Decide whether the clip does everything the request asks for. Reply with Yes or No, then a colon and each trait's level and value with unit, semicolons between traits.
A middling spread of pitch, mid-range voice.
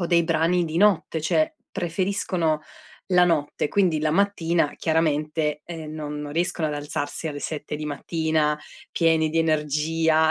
No: narrow, 2.0 semitones; medium, 160 Hz